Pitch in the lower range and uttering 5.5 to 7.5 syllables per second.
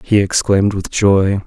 No: low, 100 Hz; 4.4 syllables/s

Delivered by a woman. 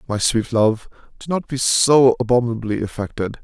No: male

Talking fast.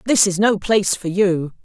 Yes: fast, 220 wpm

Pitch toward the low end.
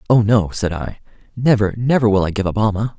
Yes: low, 105 Hz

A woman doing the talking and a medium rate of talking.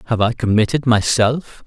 No: male; average, 145 wpm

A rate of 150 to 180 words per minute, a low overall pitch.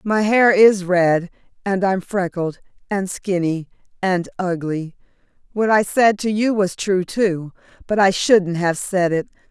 No: average, 160 wpm; high, 190 Hz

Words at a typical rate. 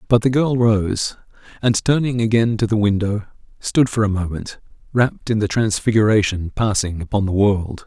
Yes: average, 170 wpm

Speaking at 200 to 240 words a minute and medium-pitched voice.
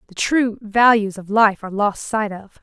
No: fast, 205 wpm; high, 210 Hz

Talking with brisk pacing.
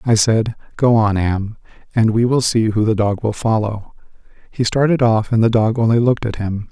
Yes: fast, 215 wpm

